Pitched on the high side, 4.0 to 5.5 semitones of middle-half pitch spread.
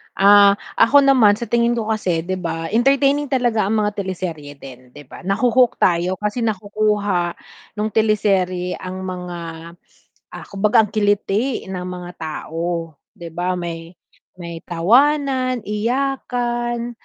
Yes: high, 205 Hz; average, 5.0 semitones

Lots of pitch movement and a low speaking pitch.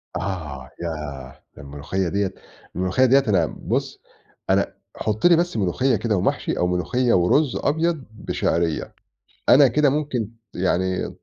Yes: wide, 7.0 semitones; low, 100 Hz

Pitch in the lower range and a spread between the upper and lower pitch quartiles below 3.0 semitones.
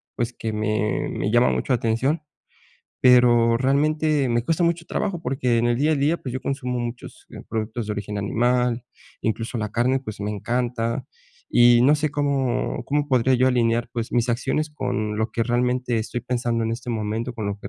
Yes: low, 120 Hz; narrow, 2.4 semitones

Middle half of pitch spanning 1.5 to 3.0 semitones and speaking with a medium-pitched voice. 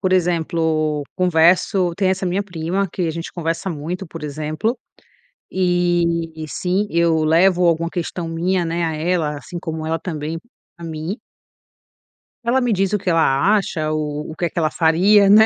Yes: narrow, 2.6 semitones; medium, 170 Hz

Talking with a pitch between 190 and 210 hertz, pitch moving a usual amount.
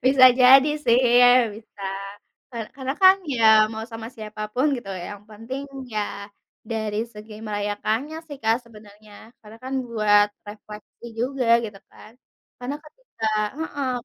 No: high, 225 Hz; average, 3.6 semitones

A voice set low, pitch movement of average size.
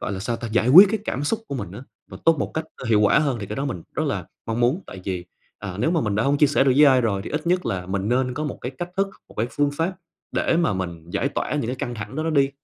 No: low, 130 Hz; wide, 6.2 semitones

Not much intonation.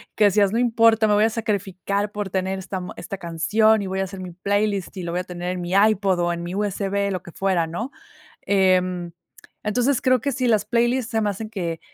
No: average, 3.0 semitones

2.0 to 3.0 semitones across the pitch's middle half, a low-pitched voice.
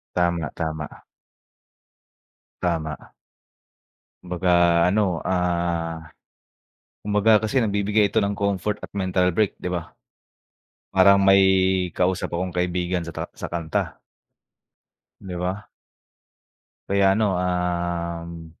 Yes: narrow, 2.5 semitones; very low, 90 Hz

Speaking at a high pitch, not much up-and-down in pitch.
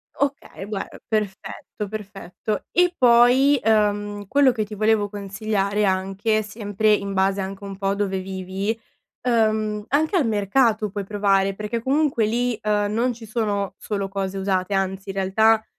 Yes: high, 210 Hz; narrow, 2.2 semitones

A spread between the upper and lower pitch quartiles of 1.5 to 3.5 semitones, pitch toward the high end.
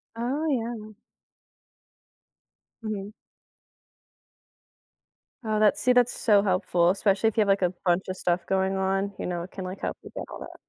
Yes: average, 2.8 semitones; high, 200 Hz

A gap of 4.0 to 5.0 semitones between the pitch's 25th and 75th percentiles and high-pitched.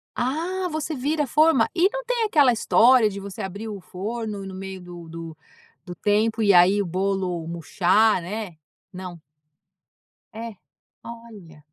Yes: average, 4.7 semitones; high, 205 Hz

